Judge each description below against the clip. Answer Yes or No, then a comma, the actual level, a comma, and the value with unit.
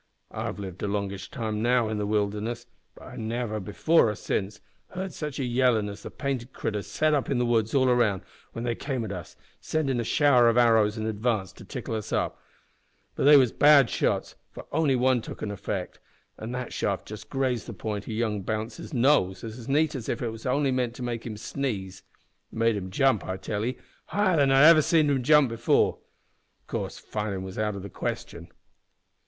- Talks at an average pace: No, fast, 210 wpm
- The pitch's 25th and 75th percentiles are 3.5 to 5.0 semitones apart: Yes, average, 4.1 semitones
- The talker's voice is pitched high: No, low, 115 Hz